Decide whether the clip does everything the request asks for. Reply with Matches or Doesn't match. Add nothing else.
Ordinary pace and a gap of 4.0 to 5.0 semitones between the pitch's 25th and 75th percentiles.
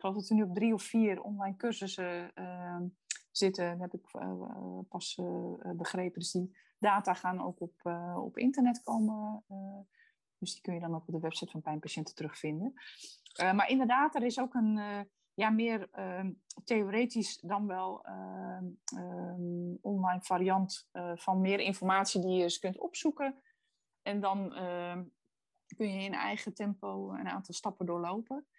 Doesn't match